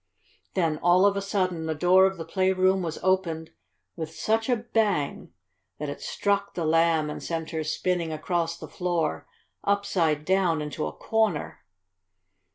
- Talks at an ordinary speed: Yes, average, 160 wpm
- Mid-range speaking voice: Yes, medium, 175 Hz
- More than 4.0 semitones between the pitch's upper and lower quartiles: No, average, 3.1 semitones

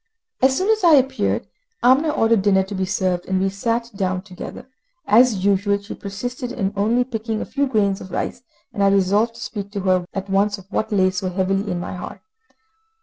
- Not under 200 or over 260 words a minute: Yes, fast, 205 wpm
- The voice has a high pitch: Yes, high, 200 Hz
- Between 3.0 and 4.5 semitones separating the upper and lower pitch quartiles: Yes, average, 3.5 semitones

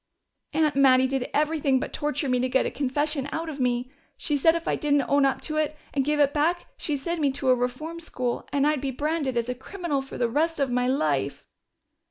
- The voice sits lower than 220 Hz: No, very high, 280 Hz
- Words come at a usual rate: No, fast, 235 wpm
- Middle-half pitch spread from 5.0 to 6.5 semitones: No, average, 2.9 semitones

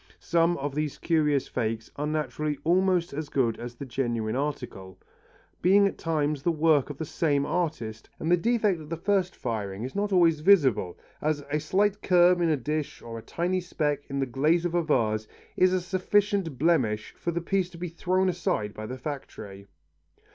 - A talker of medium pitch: Yes, medium, 155 Hz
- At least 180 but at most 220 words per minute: Yes, average, 190 wpm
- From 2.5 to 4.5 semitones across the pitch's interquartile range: No, average, 5.2 semitones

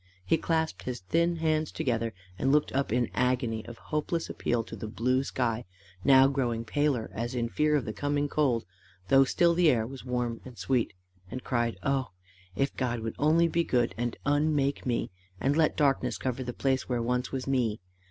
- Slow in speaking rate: No, average, 195 wpm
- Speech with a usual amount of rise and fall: Yes, average, 3.5 semitones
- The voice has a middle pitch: No, low, 130 Hz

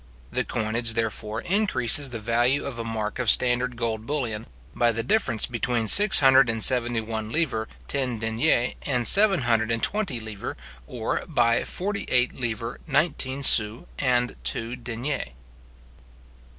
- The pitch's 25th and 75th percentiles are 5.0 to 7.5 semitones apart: No, average, 2.9 semitones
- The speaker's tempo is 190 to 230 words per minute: No, average, 150 wpm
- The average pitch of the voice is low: Yes, low, 120 Hz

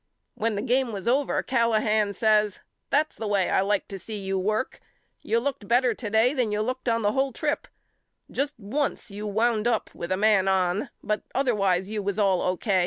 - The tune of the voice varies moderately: Yes, average, 3.3 semitones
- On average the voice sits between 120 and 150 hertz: No, high, 215 Hz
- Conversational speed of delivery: No, fast, 210 wpm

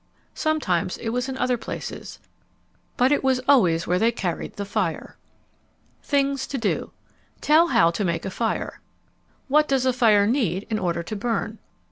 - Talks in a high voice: Yes, high, 230 Hz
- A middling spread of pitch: No, wide, 5.7 semitones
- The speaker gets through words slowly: No, average, 165 wpm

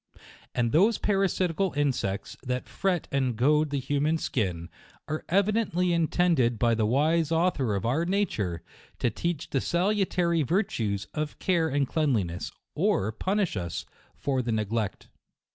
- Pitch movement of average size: No, wide, 7.0 semitones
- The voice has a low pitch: No, medium, 145 Hz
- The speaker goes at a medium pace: Yes, average, 145 wpm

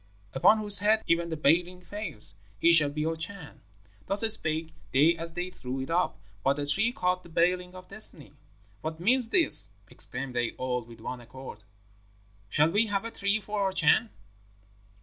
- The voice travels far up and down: Yes, wide, 5.7 semitones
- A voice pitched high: No, medium, 170 Hz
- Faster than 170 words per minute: Yes, average, 180 wpm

